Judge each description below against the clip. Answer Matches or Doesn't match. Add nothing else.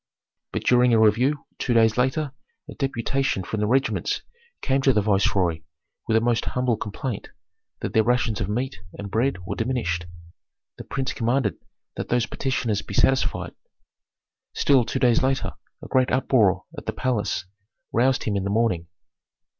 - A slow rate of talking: Doesn't match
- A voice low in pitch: Matches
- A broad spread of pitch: Doesn't match